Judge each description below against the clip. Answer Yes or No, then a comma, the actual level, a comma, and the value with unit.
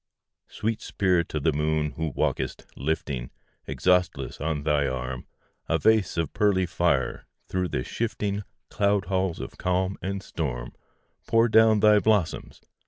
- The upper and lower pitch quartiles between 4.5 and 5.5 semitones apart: Yes, average, 5.0 semitones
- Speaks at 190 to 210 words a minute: No, average, 145 wpm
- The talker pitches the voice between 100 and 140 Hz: No, very low, 90 Hz